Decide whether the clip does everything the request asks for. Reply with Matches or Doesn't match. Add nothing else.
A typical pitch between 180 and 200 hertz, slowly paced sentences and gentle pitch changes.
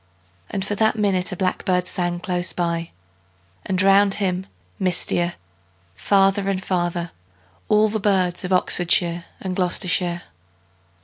Matches